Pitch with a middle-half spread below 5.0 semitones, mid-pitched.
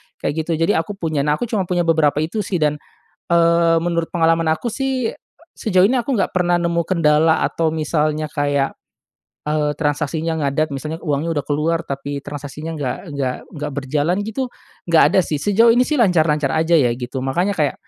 Yes: average, 2.8 semitones; medium, 160 Hz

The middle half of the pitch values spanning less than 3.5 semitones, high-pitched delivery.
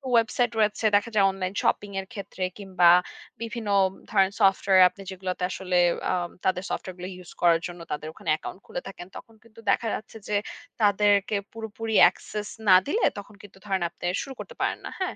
Yes: average, 3.0 semitones; high, 200 Hz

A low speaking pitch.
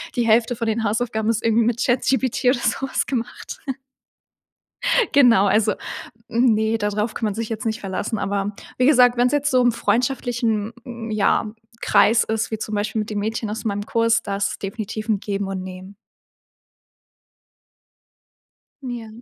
No: high, 220 Hz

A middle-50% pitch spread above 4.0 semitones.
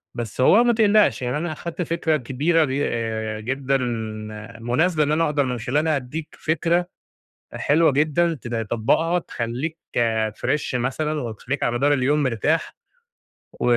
Yes: average, 4.7 semitones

